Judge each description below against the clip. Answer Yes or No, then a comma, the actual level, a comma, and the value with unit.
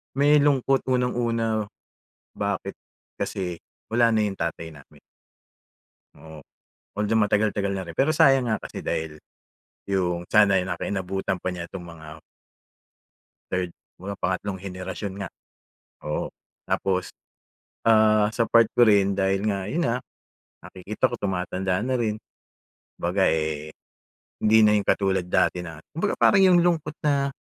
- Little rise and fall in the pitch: No, average, 4.1 semitones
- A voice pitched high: No, low, 100 Hz